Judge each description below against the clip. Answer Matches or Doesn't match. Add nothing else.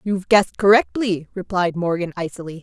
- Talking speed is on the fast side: Doesn't match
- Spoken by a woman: Matches